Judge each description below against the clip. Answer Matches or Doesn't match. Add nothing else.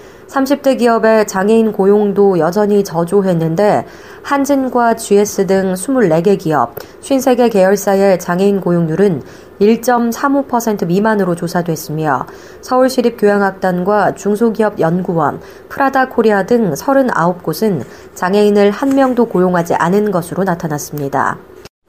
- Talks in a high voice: Matches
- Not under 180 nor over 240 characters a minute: Doesn't match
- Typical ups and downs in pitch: Matches